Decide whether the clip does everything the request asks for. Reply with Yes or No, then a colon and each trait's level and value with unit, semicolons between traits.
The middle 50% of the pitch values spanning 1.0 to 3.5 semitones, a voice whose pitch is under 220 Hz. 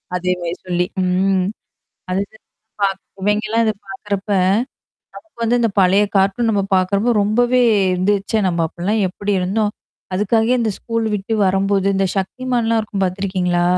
Yes: average, 3.1 semitones; high, 200 Hz